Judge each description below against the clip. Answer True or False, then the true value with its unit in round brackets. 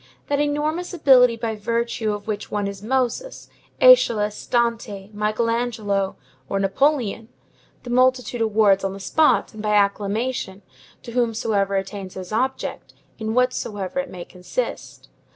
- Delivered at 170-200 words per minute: False (135 wpm)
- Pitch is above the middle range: True (220 Hz)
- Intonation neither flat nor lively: True (3.8 semitones)